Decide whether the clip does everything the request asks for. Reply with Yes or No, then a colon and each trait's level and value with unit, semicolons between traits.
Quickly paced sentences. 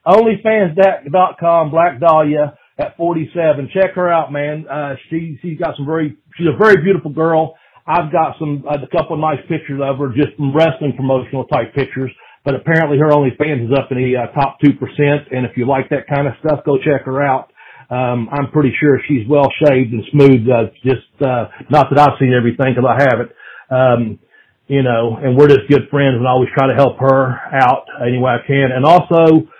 Yes: fast, 210 wpm